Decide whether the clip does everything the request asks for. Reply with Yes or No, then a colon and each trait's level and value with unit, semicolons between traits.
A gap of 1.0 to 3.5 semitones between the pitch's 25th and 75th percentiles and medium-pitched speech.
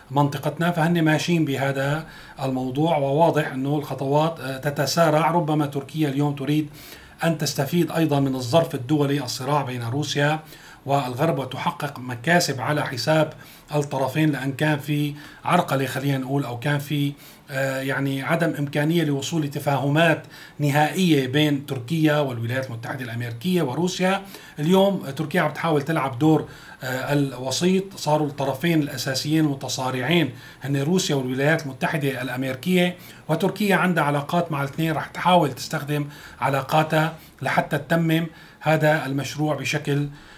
Yes: narrow, 2.6 semitones; medium, 150 Hz